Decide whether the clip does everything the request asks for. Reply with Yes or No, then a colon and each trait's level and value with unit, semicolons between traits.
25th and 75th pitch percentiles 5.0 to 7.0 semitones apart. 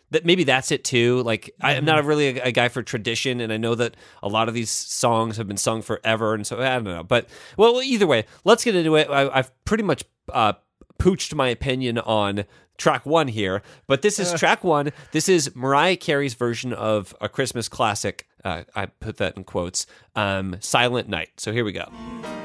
Yes: average, 5.3 semitones